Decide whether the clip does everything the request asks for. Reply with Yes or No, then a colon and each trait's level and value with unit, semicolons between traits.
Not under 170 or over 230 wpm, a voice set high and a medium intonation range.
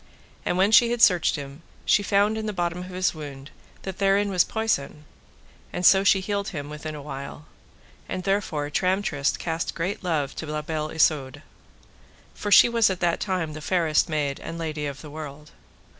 No: average, 190 wpm; medium, 165 Hz; average, 4.4 semitones